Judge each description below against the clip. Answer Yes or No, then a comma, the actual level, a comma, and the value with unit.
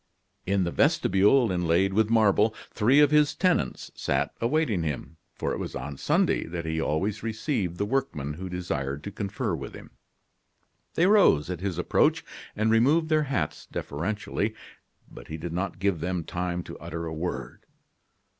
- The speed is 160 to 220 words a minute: Yes, average, 165 wpm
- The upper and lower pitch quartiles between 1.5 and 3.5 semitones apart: No, average, 5.2 semitones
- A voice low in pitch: Yes, very low, 95 Hz